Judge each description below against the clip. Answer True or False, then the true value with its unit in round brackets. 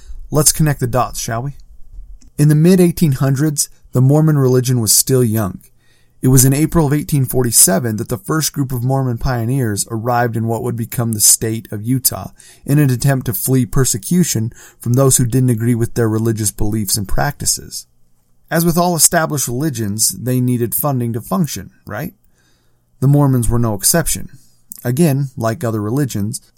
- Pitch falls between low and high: False (125 Hz)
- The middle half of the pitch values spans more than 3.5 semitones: True (4.0 semitones)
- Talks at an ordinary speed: True (170 wpm)